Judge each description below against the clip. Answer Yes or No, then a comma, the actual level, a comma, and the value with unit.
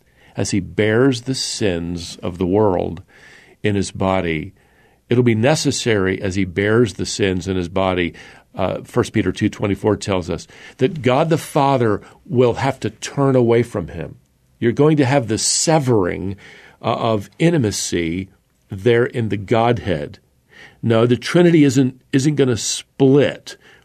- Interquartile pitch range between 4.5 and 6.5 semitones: Yes, average, 5.2 semitones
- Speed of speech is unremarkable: Yes, average, 165 wpm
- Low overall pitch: Yes, low, 110 Hz